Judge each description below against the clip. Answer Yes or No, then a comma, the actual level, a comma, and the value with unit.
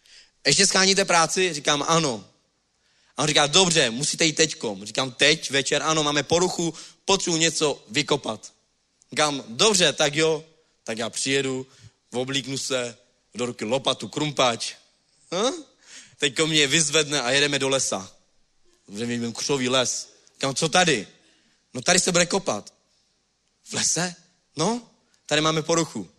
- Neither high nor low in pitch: Yes, medium, 150 Hz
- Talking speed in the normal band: Yes, average, 140 wpm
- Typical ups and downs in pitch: Yes, average, 4.0 semitones